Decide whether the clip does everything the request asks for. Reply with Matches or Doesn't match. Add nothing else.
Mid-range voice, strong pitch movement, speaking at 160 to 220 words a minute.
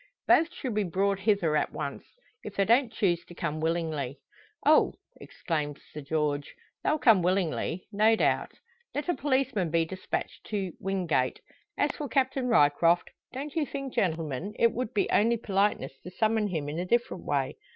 Doesn't match